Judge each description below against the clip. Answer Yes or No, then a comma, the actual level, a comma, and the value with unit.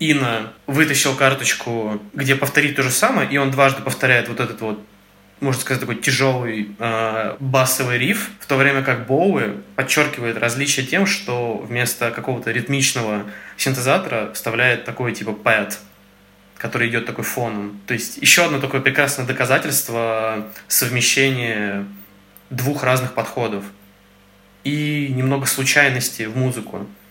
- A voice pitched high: No, low, 125 Hz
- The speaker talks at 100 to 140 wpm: Yes, average, 130 wpm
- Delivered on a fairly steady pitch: No, average, 3.5 semitones